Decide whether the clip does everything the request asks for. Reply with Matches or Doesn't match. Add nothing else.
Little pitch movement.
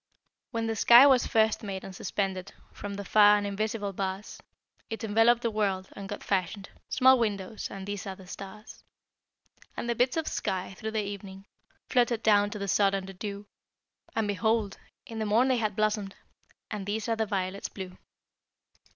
Matches